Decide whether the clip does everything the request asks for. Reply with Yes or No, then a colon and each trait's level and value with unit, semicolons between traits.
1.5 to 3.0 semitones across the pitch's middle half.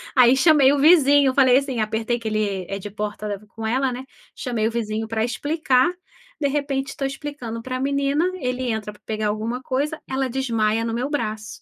No: average, 4.0 semitones